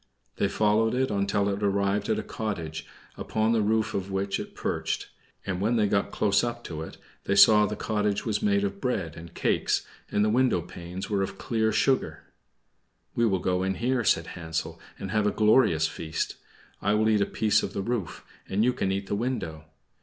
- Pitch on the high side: No, low, 100 Hz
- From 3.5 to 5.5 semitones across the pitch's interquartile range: No, narrow, 2.4 semitones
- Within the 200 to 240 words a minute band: Yes, fast, 205 wpm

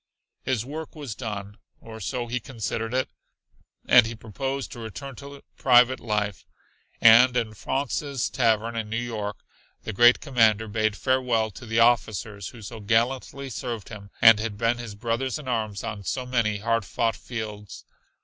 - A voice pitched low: Yes, low, 115 Hz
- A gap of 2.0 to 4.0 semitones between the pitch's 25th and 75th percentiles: Yes, narrow, 2.6 semitones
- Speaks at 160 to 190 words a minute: Yes, average, 170 wpm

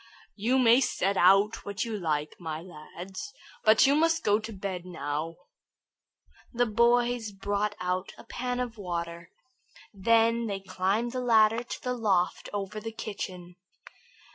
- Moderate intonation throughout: Yes, average, 4.2 semitones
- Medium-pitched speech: No, high, 205 Hz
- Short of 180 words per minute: Yes, average, 145 wpm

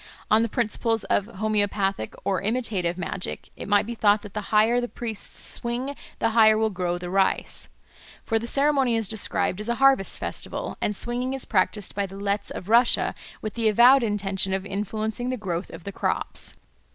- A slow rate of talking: No, average, 190 wpm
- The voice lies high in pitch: Yes, high, 215 Hz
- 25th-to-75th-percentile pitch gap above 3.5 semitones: No, average, 3.2 semitones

